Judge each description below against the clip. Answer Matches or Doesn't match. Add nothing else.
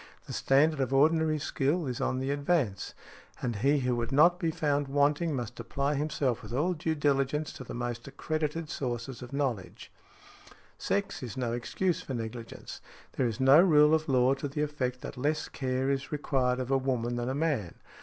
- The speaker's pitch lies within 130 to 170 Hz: Matches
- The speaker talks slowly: Doesn't match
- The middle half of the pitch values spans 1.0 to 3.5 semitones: Matches